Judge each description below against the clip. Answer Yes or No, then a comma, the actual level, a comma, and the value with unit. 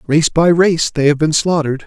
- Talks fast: Yes, fast, 225 wpm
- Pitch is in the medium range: Yes, medium, 155 Hz